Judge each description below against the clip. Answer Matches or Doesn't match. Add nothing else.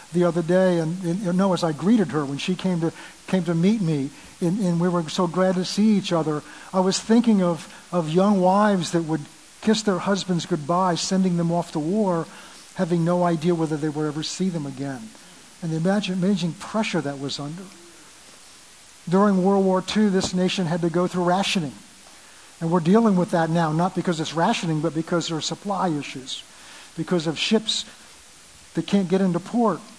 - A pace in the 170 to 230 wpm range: Matches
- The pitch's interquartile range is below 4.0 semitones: Matches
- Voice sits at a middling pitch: Matches